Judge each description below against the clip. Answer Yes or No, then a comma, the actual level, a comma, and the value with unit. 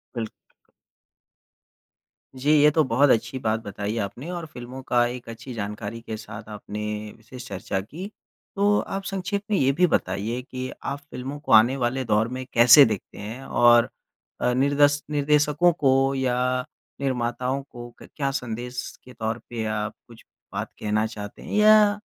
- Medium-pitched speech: No, low, 125 Hz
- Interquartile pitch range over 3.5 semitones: Yes, average, 4.0 semitones